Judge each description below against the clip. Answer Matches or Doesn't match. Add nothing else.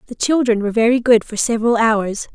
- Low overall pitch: Doesn't match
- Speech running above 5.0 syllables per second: Matches